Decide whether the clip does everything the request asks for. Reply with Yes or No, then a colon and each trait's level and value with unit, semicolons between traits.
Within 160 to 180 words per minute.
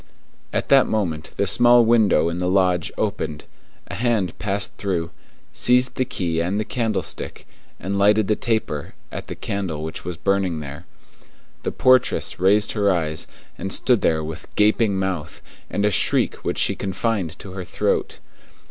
Yes: average, 165 wpm